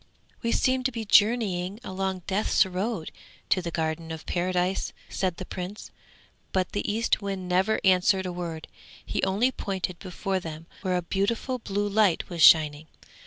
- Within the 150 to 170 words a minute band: Yes, average, 160 wpm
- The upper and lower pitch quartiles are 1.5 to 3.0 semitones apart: Yes, narrow, 2.6 semitones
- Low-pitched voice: No, high, 190 Hz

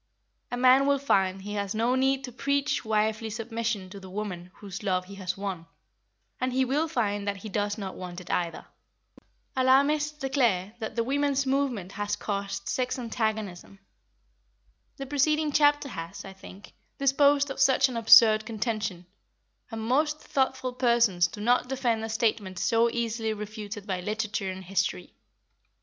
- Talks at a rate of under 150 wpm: No, average, 160 wpm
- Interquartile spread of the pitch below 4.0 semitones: No, average, 4.7 semitones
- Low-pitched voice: No, high, 225 Hz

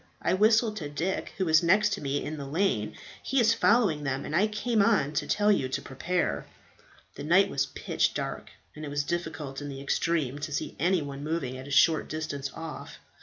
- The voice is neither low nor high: Yes, medium, 155 Hz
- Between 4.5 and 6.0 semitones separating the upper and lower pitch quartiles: Yes, wide, 5.5 semitones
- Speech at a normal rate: No, fast, 215 wpm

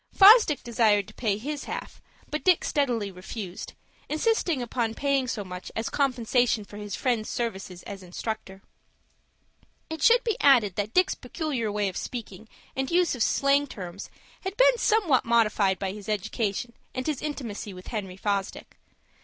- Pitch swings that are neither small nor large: No, wide, 5.9 semitones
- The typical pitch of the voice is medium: No, high, 230 Hz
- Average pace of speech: Yes, average, 160 wpm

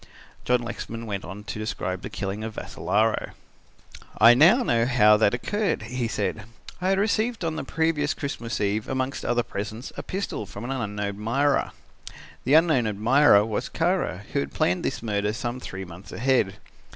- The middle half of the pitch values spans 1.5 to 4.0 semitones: No, average, 5.3 semitones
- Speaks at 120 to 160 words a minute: No, average, 175 wpm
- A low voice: Yes, low, 115 Hz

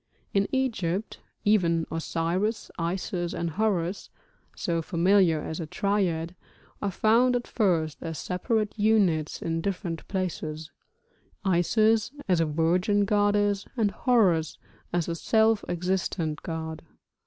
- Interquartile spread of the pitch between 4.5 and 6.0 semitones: No, average, 3.9 semitones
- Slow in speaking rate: Yes, slow, 120 wpm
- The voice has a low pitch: No, medium, 180 Hz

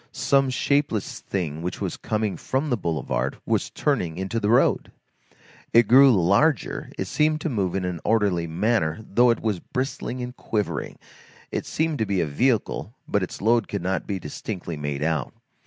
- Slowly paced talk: No, average, 175 wpm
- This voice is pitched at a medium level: No, low, 105 Hz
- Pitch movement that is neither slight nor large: No, wide, 5.7 semitones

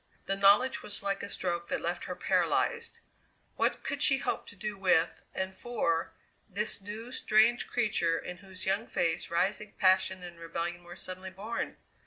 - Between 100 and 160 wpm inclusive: No, average, 170 wpm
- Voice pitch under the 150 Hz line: No, high, 190 Hz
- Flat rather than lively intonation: No, average, 3.2 semitones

